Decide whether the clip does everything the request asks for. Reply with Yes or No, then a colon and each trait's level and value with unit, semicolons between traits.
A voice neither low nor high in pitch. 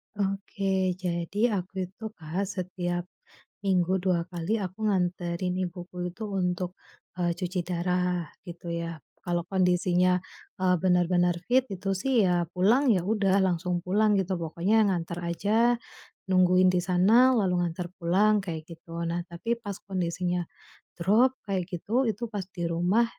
Yes: medium, 180 Hz